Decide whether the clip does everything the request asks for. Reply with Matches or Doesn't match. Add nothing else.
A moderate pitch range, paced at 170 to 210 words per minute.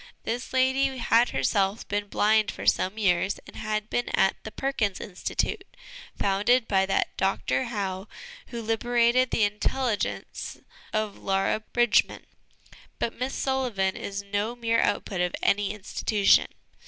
Doesn't match